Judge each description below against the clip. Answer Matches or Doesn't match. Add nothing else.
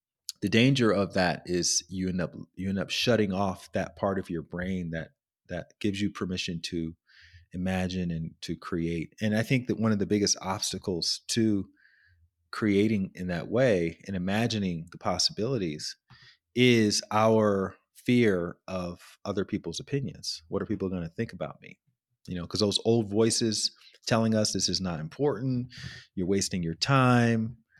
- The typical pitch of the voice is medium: Doesn't match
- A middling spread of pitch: Matches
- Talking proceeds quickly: Doesn't match